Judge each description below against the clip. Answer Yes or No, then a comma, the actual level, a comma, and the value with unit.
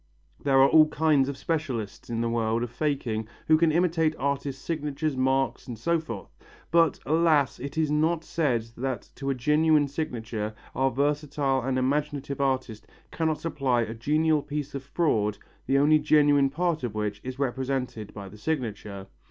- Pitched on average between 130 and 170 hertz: Yes, medium, 140 Hz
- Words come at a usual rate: Yes, average, 170 wpm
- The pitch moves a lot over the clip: No, average, 4.1 semitones